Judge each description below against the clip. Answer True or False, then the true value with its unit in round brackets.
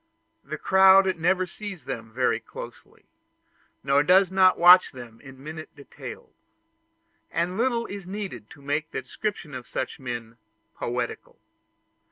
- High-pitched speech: False (160 Hz)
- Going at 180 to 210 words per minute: False (135 wpm)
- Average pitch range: False (6.6 semitones)